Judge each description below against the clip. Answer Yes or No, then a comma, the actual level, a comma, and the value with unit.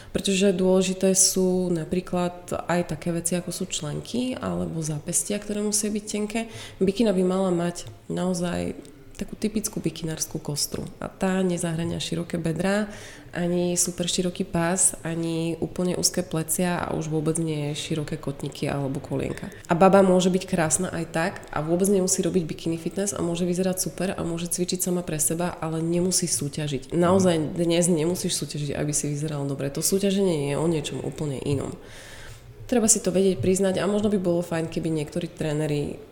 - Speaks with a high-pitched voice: No, medium, 175 Hz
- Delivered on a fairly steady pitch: No, average, 3.0 semitones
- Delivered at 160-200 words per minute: Yes, average, 165 wpm